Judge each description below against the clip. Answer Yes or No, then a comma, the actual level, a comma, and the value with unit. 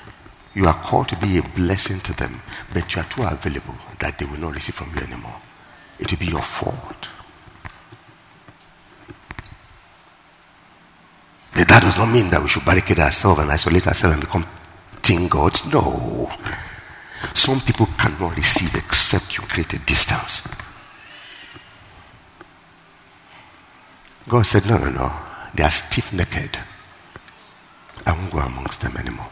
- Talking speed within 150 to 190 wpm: No, slow, 135 wpm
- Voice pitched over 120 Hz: No, very low, 90 Hz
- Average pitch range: Yes, average, 4.3 semitones